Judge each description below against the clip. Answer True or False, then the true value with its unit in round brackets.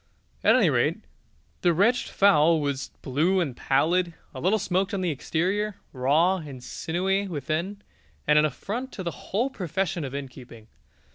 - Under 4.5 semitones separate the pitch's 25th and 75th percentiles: False (5.1 semitones)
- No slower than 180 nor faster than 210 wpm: False (155 wpm)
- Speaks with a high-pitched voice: False (170 Hz)